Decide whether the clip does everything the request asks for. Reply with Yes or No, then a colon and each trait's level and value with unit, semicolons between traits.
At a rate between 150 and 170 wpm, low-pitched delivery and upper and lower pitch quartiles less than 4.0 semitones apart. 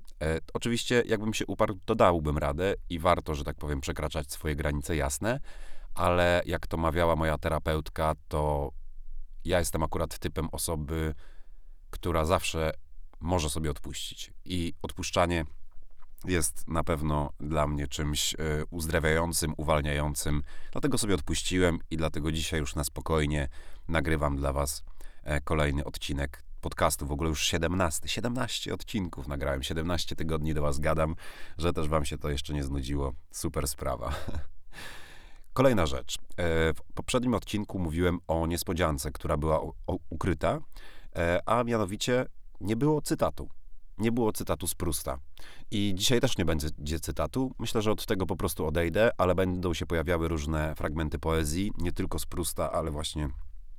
No: average, 140 wpm; very low, 80 Hz; average, 2.9 semitones